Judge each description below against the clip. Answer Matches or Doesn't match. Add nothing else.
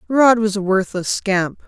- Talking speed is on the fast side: Doesn't match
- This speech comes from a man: Doesn't match